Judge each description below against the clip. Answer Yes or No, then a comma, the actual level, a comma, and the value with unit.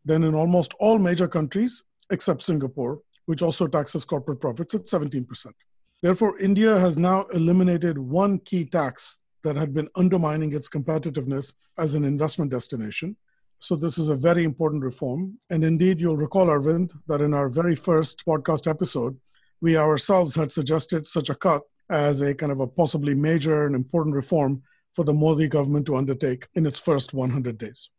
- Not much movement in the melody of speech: No, average, 3.2 semitones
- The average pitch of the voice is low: No, medium, 160 Hz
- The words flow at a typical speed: Yes, average, 170 wpm